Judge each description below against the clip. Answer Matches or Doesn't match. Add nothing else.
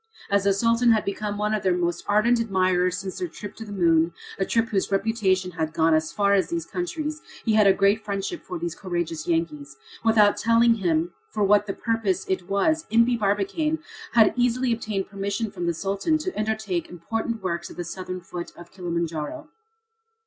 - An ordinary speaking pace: Matches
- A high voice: Matches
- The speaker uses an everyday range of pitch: Matches